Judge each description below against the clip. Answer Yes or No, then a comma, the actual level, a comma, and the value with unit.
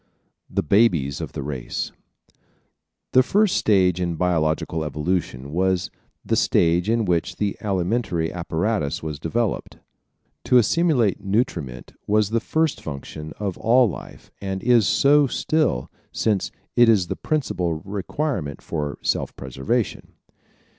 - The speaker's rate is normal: No, slow, 130 wpm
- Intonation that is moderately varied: No, wide, 6.4 semitones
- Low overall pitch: Yes, very low, 95 Hz